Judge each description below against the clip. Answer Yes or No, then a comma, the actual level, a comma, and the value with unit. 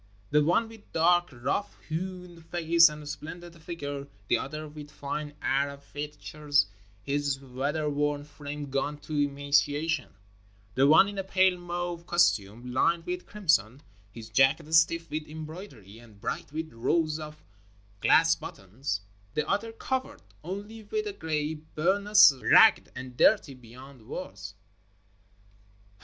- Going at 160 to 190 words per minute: No, average, 140 wpm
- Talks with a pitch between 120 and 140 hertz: No, medium, 150 Hz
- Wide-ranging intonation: No, average, 3.7 semitones